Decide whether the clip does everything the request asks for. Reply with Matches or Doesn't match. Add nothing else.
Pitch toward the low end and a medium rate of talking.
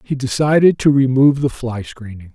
Matches